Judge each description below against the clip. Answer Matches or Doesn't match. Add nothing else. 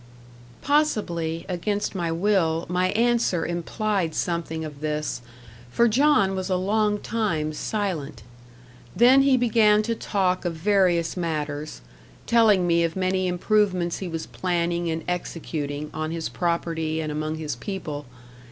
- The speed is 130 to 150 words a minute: Matches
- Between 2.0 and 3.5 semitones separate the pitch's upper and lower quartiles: Doesn't match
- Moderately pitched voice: Matches